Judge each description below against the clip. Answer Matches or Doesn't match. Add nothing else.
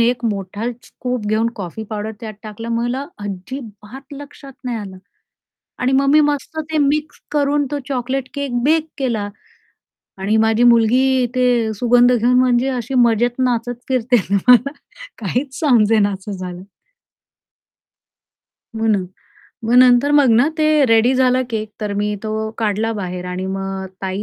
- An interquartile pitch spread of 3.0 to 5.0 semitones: Matches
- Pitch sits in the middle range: Doesn't match